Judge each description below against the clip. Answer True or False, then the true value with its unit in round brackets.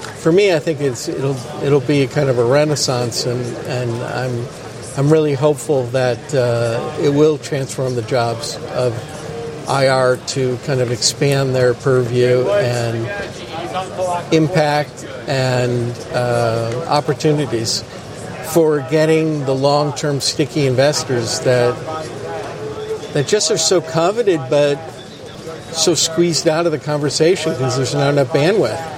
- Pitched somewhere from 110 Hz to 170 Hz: True (140 Hz)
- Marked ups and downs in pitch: False (3.9 semitones)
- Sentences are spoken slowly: True (130 wpm)